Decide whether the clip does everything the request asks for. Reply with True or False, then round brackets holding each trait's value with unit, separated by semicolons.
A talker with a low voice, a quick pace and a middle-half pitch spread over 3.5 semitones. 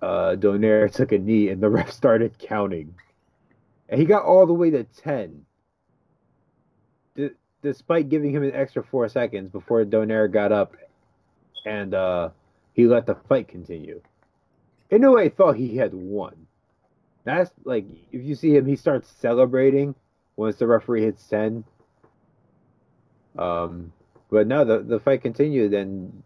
False (110 Hz; 150 wpm; 4.9 semitones)